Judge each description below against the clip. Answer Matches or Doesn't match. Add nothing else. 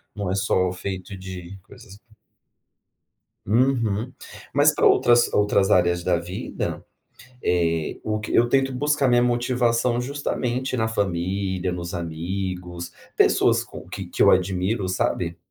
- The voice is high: Doesn't match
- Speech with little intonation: Doesn't match